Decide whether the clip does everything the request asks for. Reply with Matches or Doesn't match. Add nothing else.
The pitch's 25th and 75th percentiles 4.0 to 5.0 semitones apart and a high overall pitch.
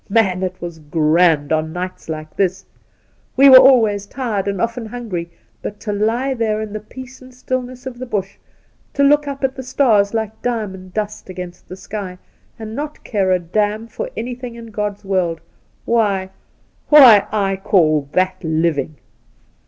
Matches